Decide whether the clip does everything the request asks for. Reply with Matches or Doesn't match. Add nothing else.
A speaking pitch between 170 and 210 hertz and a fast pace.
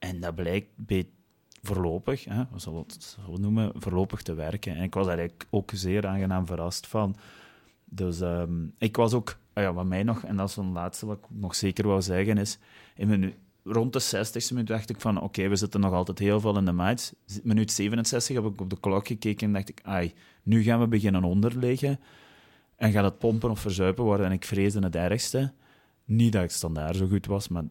Doesn't match